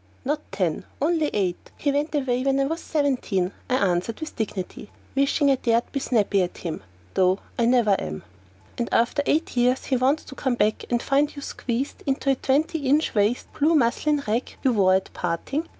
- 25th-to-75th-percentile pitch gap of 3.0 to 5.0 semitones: No, wide, 5.4 semitones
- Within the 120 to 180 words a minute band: No, average, 195 wpm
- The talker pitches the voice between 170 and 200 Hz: No, very high, 255 Hz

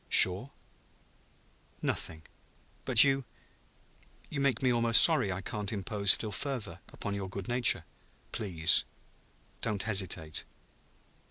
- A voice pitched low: Yes, low, 105 Hz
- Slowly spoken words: Yes, slow, 110 wpm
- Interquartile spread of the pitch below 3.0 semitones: No, average, 4.4 semitones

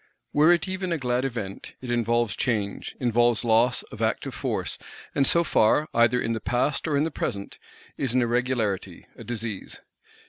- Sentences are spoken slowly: No, average, 175 wpm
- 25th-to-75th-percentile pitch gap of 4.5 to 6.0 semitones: No, average, 3.3 semitones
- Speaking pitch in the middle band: No, low, 120 Hz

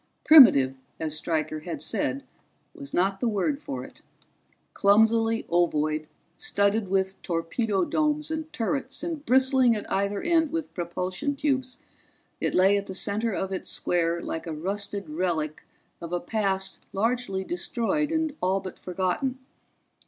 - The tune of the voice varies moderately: No, wide, 6.7 semitones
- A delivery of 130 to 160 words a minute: Yes, average, 145 wpm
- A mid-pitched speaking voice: No, high, 200 Hz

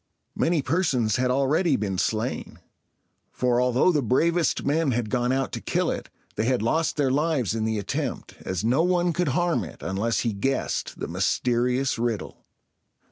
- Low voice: Yes, low, 125 Hz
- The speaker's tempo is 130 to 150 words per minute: No, average, 170 wpm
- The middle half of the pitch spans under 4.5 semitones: No, average, 5.2 semitones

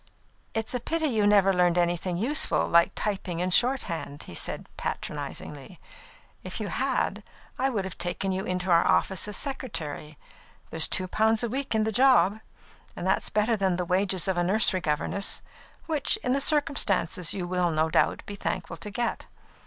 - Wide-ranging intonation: No, average, 4.3 semitones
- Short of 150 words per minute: No, average, 180 wpm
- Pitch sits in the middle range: No, high, 195 Hz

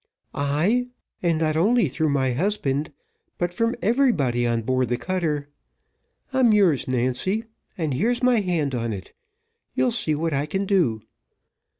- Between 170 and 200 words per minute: No, average, 150 wpm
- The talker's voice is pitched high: No, medium, 155 Hz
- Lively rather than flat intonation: Yes, wide, 7.5 semitones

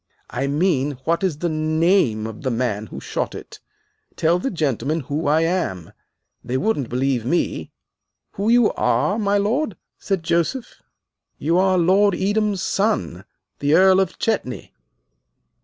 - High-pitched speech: No, medium, 165 Hz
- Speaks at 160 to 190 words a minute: No, average, 145 wpm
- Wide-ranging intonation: Yes, wide, 6.2 semitones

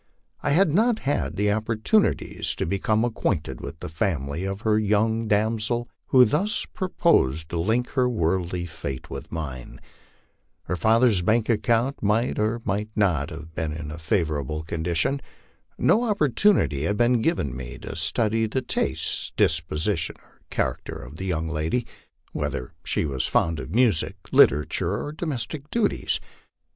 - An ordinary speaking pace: Yes, average, 150 wpm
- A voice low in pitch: Yes, low, 105 Hz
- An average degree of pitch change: No, wide, 6.9 semitones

